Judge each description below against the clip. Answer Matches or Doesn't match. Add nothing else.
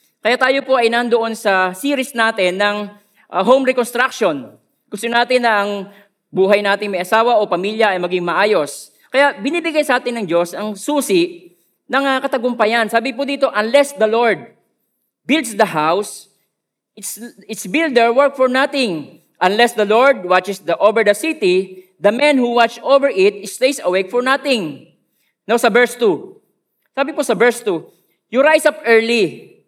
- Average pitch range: Matches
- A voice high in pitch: Matches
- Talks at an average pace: Doesn't match